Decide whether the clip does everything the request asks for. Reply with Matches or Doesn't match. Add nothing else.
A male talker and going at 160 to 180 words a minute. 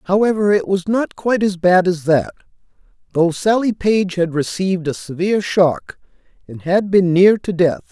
Matches